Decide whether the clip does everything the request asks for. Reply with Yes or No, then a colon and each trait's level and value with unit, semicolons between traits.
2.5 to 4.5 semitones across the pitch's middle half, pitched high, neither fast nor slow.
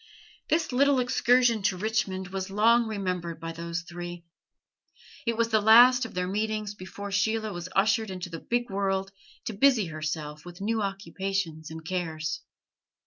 Yes: average, 4.1 semitones; high, 195 Hz; average, 155 wpm